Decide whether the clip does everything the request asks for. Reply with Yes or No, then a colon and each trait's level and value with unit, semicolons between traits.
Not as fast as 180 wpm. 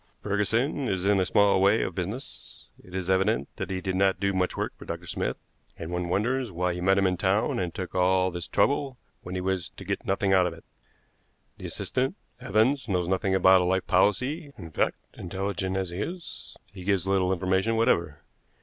No: fast, 205 wpm